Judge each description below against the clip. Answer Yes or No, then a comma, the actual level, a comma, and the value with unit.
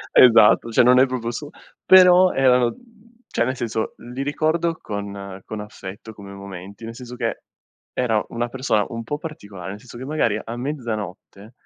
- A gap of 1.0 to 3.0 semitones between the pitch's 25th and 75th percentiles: No, average, 4.1 semitones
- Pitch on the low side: Yes, low, 115 Hz